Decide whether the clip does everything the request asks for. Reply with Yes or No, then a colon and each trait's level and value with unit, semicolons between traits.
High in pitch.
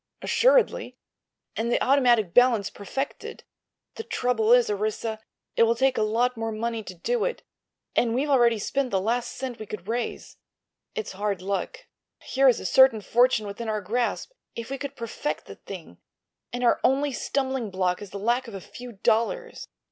Yes: high, 235 Hz